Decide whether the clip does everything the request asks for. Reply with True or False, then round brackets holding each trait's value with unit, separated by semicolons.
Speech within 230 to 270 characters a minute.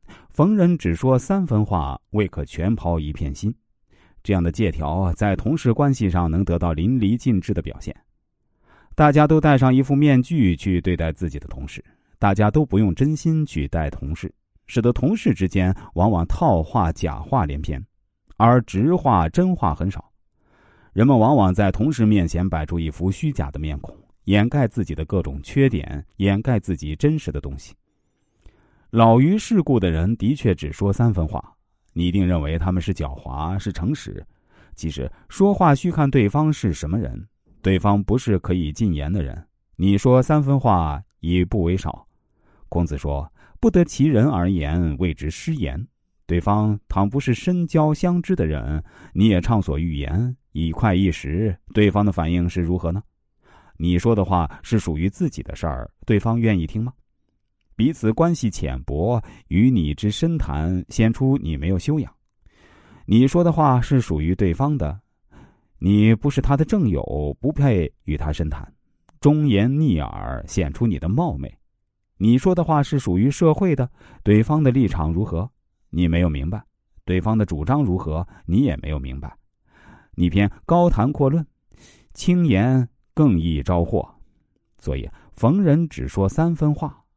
True (235 characters per minute)